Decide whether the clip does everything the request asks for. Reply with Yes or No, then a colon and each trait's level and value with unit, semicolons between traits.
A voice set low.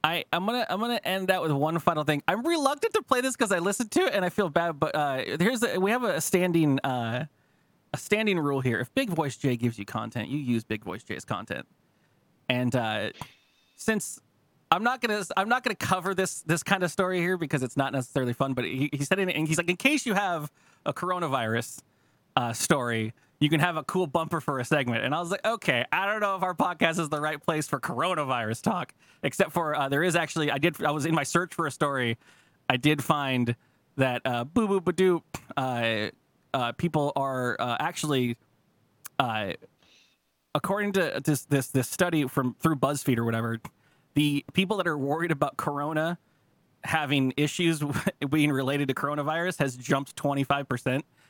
No: medium, 150 Hz